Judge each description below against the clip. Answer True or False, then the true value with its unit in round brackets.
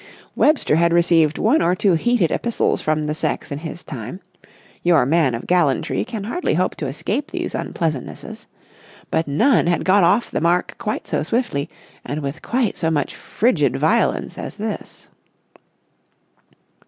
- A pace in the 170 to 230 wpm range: False (150 wpm)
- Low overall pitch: False (170 Hz)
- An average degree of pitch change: False (5.9 semitones)